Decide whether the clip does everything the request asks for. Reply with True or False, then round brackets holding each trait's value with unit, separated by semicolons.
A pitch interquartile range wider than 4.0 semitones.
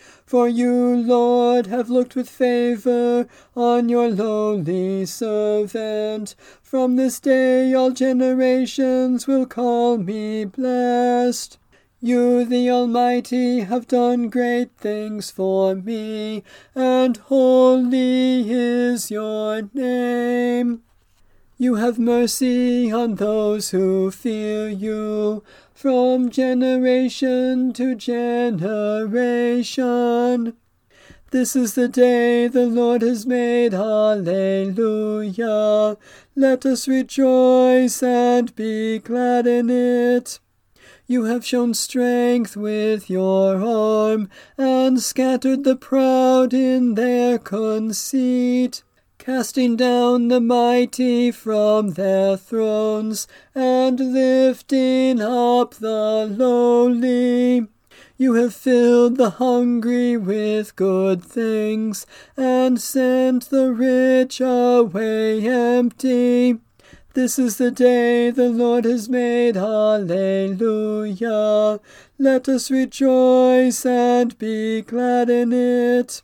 False (2.6 semitones)